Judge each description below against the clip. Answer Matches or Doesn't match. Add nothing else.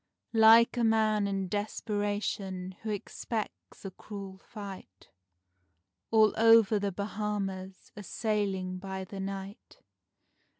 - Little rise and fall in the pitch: Matches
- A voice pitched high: Matches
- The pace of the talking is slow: Matches